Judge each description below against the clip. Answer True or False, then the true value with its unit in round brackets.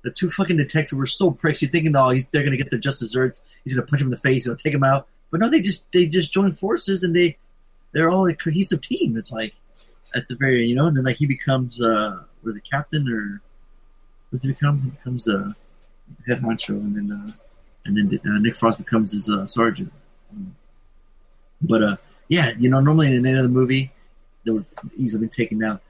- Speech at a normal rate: False (235 wpm)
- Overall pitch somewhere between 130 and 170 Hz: True (135 Hz)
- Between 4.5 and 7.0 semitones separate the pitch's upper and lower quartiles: True (5.4 semitones)